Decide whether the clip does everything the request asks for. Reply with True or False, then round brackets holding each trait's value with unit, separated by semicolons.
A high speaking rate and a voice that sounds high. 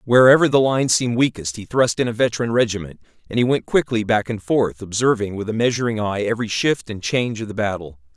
False (220 wpm; 110 Hz)